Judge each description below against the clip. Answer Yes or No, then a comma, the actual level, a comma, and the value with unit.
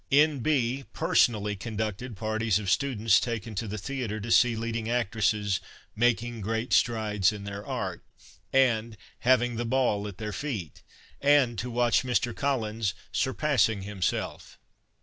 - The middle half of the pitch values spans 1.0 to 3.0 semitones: Yes, average, 2.7 semitones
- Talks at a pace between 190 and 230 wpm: No, average, 160 wpm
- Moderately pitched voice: No, low, 115 Hz